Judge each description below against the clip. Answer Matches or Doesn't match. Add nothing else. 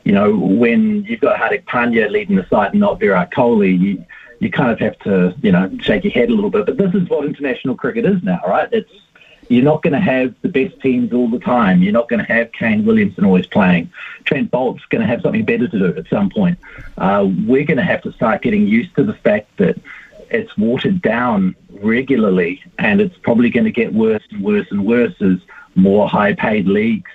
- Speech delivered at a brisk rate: Matches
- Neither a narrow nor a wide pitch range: Doesn't match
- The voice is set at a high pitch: Matches